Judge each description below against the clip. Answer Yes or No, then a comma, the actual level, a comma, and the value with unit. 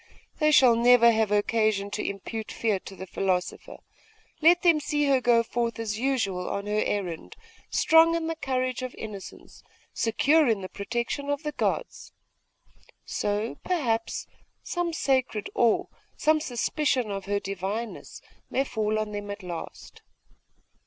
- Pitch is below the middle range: No, high, 230 Hz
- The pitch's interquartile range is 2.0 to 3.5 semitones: No, average, 5.2 semitones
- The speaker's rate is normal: Yes, average, 145 wpm